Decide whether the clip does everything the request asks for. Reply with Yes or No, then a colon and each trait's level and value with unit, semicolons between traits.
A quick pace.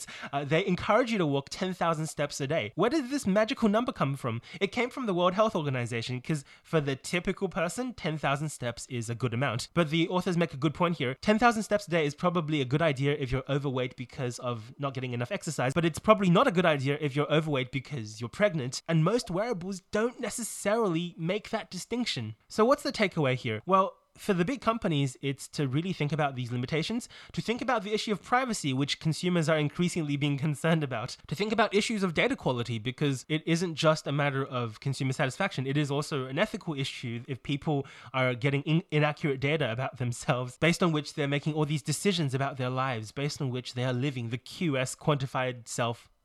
Yes: fast, 215 wpm